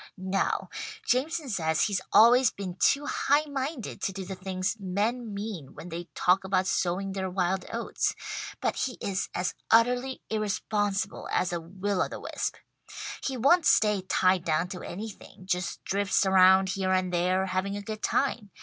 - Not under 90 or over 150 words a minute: No, average, 170 wpm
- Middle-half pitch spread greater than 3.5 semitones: No, average, 3.1 semitones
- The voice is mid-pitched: No, high, 195 Hz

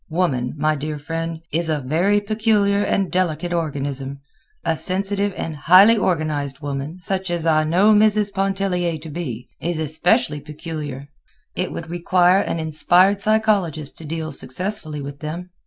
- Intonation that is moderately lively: Yes, average, 4.2 semitones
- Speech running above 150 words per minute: No, average, 145 wpm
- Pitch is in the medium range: Yes, medium, 165 Hz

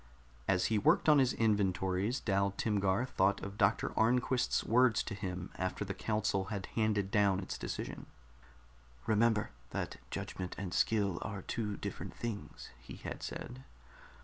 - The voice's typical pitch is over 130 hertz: No, low, 100 Hz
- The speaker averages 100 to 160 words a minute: Yes, average, 145 wpm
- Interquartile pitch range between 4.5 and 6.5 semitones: No, average, 2.7 semitones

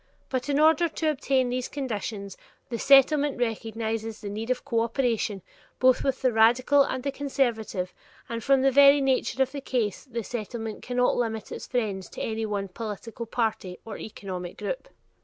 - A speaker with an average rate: Yes, average, 170 wpm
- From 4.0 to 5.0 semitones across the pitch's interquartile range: No, average, 3.4 semitones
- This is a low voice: No, high, 235 Hz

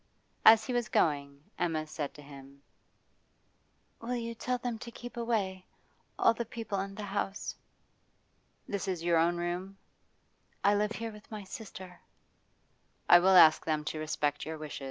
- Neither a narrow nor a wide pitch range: No, wide, 5.9 semitones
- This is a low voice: No, high, 190 Hz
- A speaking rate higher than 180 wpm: No, average, 160 wpm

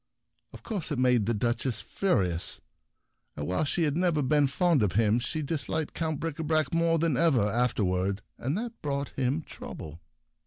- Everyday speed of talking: Yes, average, 165 wpm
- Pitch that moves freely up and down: Yes, wide, 6.1 semitones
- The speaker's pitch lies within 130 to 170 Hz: Yes, medium, 140 Hz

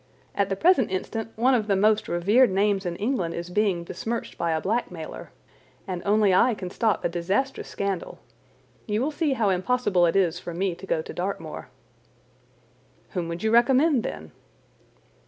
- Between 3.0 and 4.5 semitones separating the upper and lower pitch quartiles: No, average, 4.9 semitones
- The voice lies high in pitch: Yes, high, 200 Hz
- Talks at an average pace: Yes, average, 175 wpm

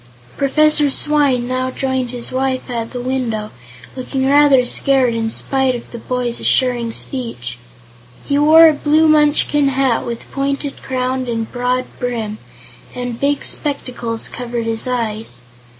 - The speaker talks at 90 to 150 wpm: Yes, average, 140 wpm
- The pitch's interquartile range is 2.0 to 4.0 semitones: Yes, average, 2.7 semitones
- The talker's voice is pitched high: Yes, very high, 255 Hz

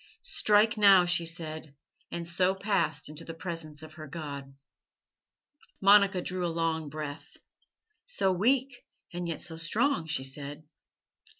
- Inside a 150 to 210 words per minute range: No, slow, 135 wpm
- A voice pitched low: No, medium, 170 Hz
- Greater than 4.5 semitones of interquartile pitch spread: No, average, 3.7 semitones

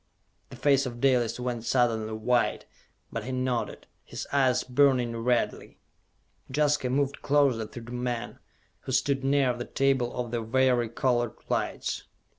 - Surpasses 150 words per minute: No, average, 145 wpm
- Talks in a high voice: No, low, 125 Hz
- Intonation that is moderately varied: No, narrow, 2.1 semitones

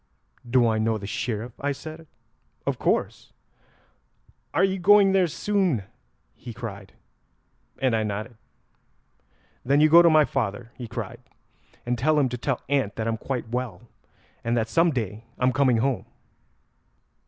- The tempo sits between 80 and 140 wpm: No, average, 155 wpm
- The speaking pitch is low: Yes, low, 125 Hz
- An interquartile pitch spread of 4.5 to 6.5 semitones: Yes, average, 5.2 semitones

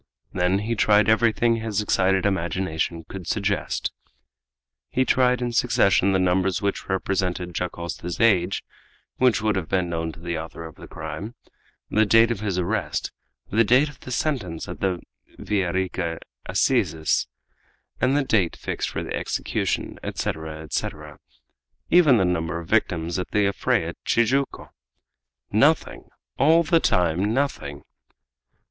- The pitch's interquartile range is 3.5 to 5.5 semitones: Yes, average, 5.1 semitones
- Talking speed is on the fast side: No, average, 140 wpm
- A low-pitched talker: Yes, very low, 95 Hz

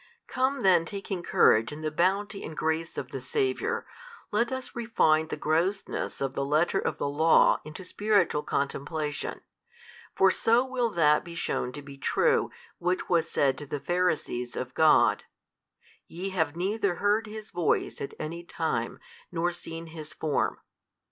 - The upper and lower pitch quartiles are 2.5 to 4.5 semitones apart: No, average, 5.0 semitones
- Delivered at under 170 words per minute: Yes, average, 160 wpm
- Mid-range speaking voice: Yes, medium, 170 Hz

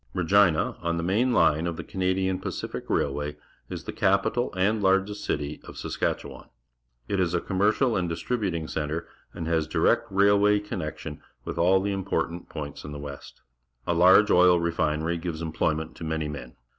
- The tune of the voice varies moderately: Yes, average, 3.6 semitones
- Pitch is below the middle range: Yes, very low, 85 Hz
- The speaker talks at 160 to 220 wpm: Yes, average, 170 wpm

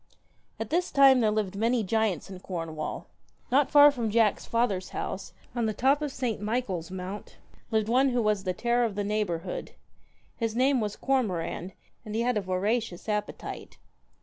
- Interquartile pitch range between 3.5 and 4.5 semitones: Yes, average, 4.1 semitones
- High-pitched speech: Yes, high, 220 Hz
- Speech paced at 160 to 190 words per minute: Yes, average, 175 wpm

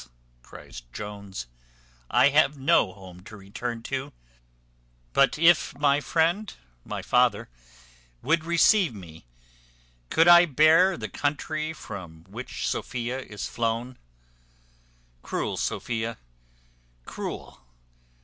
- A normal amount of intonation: No, wide, 7.2 semitones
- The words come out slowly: Yes, slow, 100 wpm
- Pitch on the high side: No, low, 130 Hz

